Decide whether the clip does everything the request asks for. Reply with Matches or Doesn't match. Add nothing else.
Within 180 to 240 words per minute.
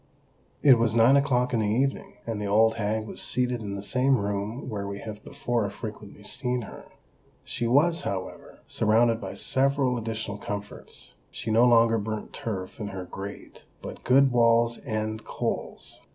Doesn't match